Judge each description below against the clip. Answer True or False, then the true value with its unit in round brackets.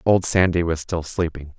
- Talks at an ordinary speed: True (190 wpm)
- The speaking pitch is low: True (85 Hz)